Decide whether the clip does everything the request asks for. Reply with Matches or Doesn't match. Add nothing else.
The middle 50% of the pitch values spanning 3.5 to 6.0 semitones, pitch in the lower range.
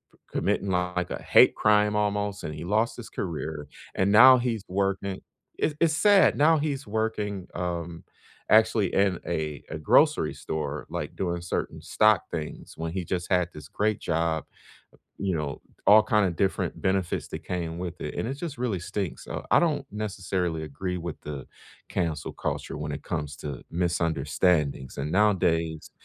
Matches